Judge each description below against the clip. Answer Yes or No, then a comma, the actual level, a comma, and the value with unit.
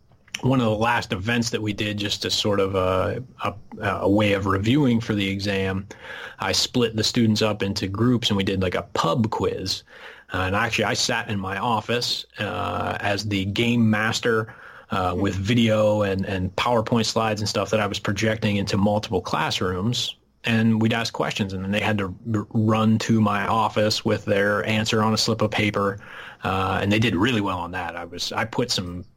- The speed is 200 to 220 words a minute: Yes, fast, 205 wpm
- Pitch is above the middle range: No, low, 105 Hz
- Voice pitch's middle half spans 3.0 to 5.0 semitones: No, narrow, 2.4 semitones